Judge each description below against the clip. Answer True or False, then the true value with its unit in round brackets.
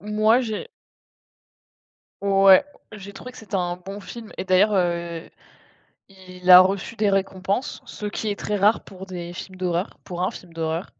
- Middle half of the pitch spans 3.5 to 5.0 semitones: False (2.4 semitones)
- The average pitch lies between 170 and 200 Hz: True (190 Hz)